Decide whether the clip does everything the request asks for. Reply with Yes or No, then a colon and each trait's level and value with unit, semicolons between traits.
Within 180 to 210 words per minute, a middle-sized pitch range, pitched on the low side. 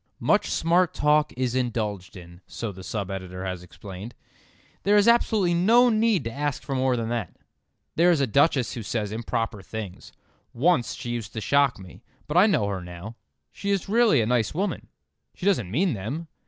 No: average, 190 wpm; wide, 8.7 semitones; low, 120 Hz